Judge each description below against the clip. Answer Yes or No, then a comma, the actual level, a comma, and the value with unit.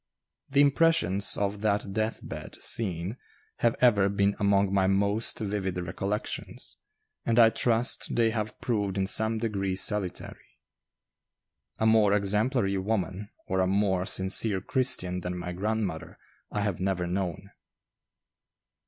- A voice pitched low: Yes, low, 100 Hz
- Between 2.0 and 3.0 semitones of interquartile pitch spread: Yes, narrow, 2.6 semitones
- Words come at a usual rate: No, slow, 130 wpm